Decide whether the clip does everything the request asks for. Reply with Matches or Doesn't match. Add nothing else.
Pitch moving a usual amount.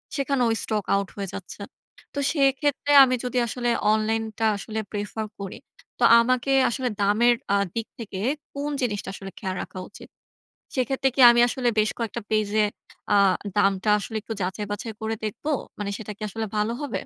Matches